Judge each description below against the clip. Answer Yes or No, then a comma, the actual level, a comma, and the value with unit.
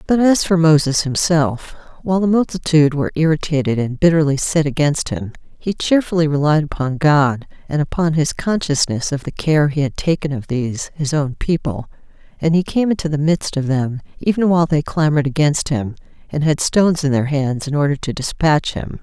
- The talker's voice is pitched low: No, medium, 150 Hz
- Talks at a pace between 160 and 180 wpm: No, average, 190 wpm